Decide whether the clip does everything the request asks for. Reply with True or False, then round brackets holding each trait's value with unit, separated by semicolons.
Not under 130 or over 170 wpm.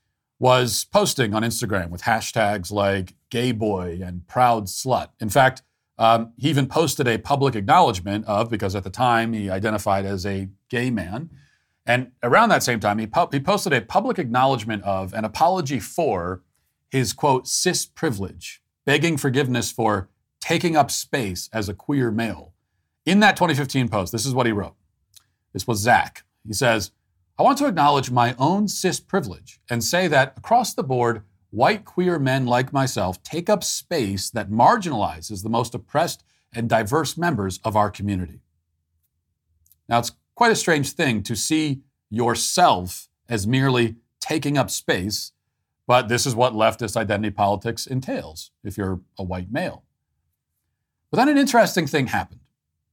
True (160 wpm)